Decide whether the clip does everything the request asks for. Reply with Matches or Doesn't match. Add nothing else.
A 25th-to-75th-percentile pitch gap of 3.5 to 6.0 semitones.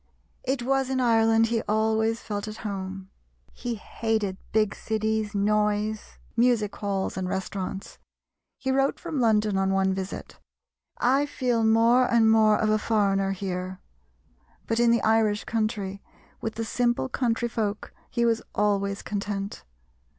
Doesn't match